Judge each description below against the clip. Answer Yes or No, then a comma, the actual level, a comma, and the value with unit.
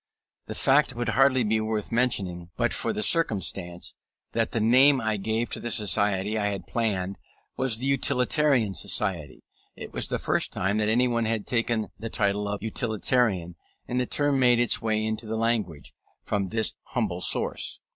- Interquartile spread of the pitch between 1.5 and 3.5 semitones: Yes, average, 2.9 semitones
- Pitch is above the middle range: No, low, 110 Hz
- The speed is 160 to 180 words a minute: Yes, average, 175 wpm